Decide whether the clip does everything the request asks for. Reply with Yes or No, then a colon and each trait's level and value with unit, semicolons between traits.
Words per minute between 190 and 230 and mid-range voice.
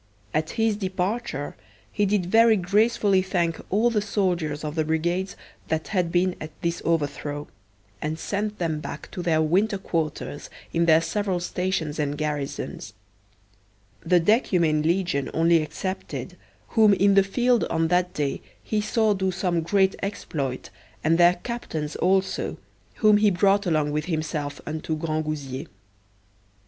No: average, 145 wpm; medium, 175 Hz